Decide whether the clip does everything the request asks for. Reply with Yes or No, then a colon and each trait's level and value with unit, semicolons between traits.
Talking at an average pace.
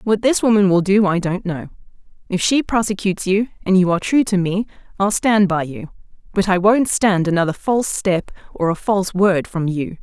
No: fast, 210 wpm